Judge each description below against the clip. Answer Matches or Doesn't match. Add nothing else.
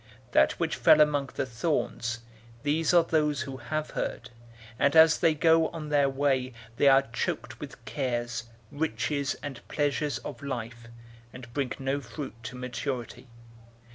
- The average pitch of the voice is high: Doesn't match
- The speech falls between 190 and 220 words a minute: Doesn't match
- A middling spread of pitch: Matches